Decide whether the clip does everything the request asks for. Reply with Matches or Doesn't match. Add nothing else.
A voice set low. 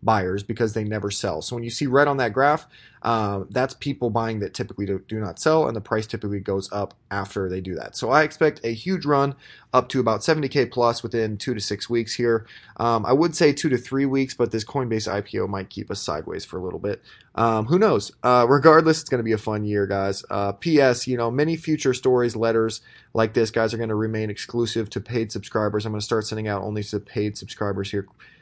Matches